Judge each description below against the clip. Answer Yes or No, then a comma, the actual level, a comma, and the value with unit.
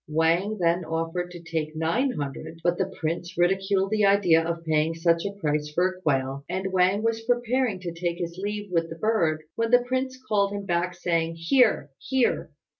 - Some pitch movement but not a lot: Yes, average, 3.8 semitones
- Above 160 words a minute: Yes, average, 190 wpm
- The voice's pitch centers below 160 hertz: No, medium, 175 Hz